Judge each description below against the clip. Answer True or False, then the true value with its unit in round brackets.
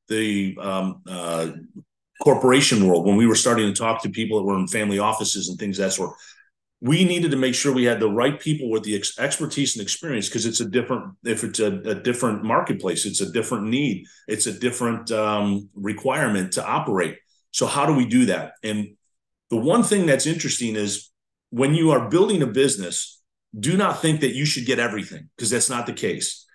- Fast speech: True (210 wpm)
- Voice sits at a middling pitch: False (115 Hz)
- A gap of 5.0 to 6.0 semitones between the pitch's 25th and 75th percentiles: True (5.5 semitones)